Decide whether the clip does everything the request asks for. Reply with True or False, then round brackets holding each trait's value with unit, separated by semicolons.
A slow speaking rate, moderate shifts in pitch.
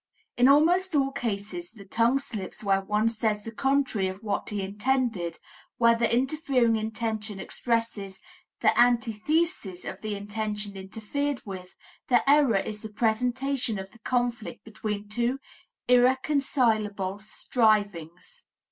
True (130 wpm; 3.6 semitones)